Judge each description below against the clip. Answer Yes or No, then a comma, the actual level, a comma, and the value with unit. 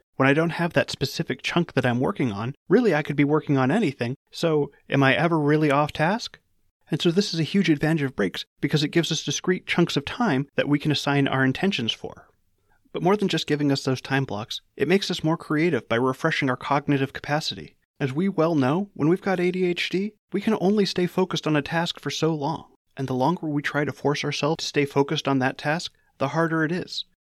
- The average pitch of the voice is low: No, medium, 150 Hz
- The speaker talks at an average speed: No, fast, 230 wpm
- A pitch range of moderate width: Yes, average, 3.7 semitones